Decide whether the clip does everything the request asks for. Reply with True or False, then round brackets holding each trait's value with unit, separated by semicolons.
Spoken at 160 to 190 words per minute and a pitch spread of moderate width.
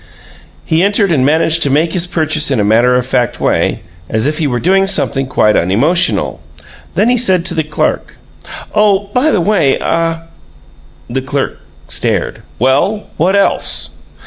False (170 wpm; 6.2 semitones)